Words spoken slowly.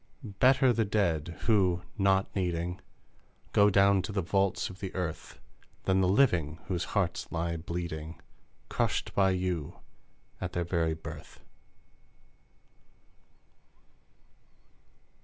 Yes: slow, 110 wpm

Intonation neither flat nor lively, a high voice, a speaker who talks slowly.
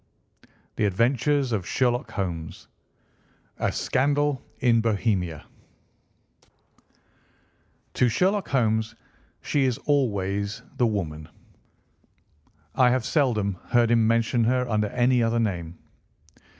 No: average, 4.0 semitones; low, 115 Hz; slow, 110 wpm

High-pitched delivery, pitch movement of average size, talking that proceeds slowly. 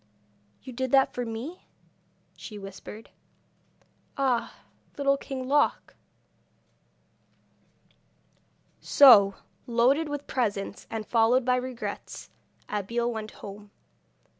Yes: high, 240 Hz; average, 3.6 semitones; slow, 95 wpm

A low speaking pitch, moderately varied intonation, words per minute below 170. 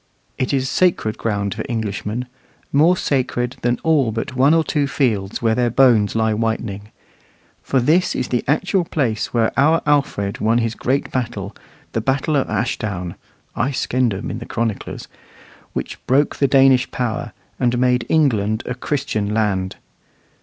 Yes: low, 120 Hz; average, 3.7 semitones; average, 155 wpm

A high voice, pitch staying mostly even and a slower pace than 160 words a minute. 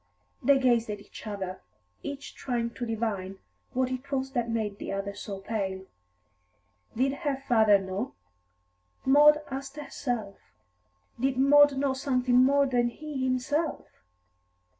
No: very high, 250 Hz; average, 4.3 semitones; slow, 135 wpm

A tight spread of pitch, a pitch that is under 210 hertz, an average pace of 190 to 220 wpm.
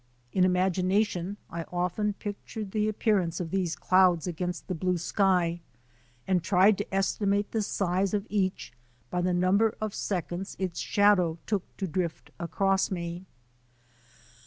No: narrow, 2.3 semitones; medium, 185 Hz; average, 145 wpm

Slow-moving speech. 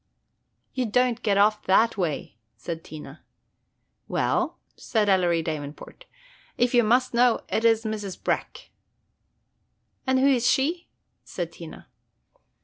Yes: slow, 125 wpm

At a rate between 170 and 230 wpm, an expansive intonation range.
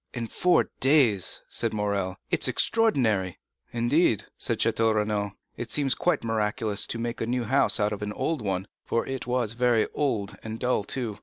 No: average, 180 wpm; average, 3.4 semitones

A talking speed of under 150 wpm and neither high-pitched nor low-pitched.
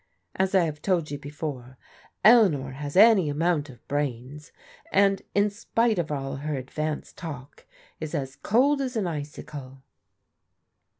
Yes: average, 140 wpm; medium, 150 Hz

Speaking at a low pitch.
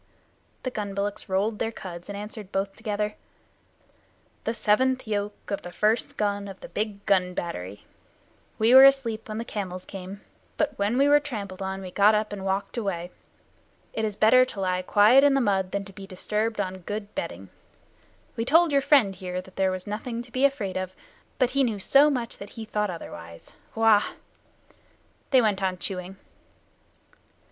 No: high, 205 Hz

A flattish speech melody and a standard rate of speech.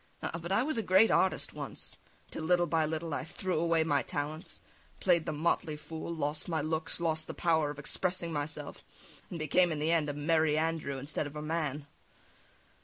Yes: narrow, 2.1 semitones; average, 195 wpm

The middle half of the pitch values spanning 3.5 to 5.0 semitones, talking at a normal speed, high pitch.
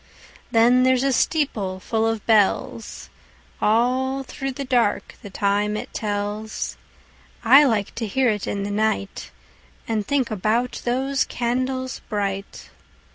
No: average, 3.8 semitones; slow, 120 wpm; high, 225 Hz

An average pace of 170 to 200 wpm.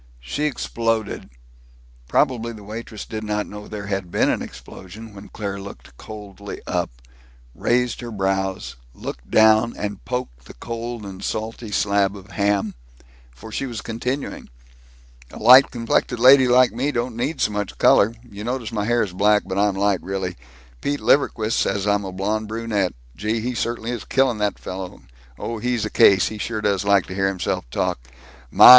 Yes: average, 175 wpm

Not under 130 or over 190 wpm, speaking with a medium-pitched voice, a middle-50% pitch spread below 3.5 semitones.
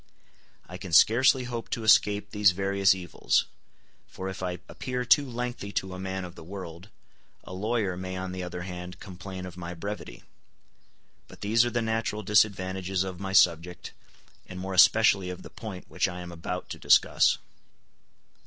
No: average, 170 wpm; very low, 95 Hz; narrow, 2.6 semitones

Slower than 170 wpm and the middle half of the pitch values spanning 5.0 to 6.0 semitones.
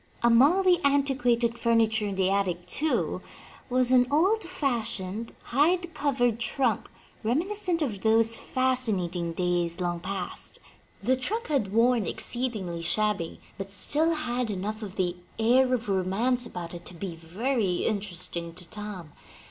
Yes: average, 140 wpm; wide, 5.5 semitones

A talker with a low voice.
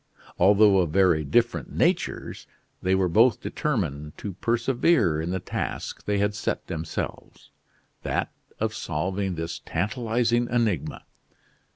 Yes: very low, 95 Hz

